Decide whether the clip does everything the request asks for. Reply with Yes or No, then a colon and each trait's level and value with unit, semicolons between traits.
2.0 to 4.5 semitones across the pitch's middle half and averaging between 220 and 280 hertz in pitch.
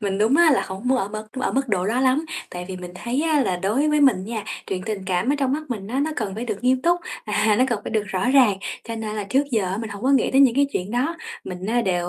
No: average, 5.2 semitones; high, 225 Hz